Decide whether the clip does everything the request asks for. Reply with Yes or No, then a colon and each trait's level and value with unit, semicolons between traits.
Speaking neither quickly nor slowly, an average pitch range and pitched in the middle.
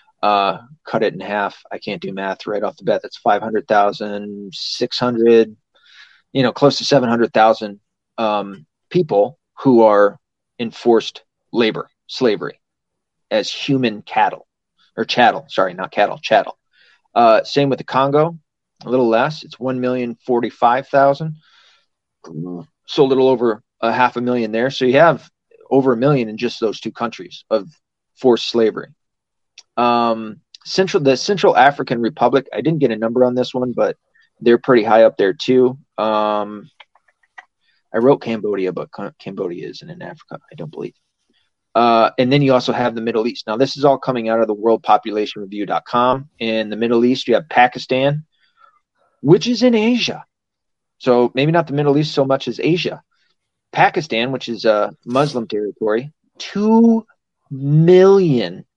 No: average, 155 wpm; average, 3.8 semitones; low, 125 Hz